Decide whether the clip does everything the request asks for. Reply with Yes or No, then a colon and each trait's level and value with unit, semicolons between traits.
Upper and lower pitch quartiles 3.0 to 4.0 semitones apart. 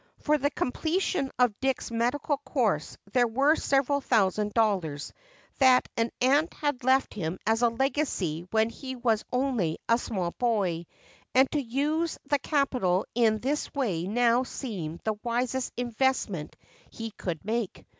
No: average, 4.4 semitones